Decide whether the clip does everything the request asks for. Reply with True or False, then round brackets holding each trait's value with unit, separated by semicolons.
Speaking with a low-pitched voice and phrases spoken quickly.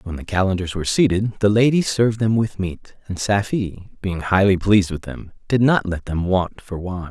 True (100 Hz; 210 wpm)